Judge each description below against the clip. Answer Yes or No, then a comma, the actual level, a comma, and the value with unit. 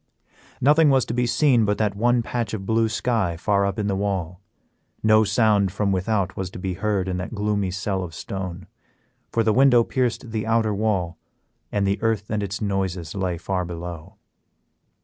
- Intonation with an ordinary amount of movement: Yes, average, 3.0 semitones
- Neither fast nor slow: Yes, average, 190 wpm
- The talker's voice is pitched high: No, low, 100 Hz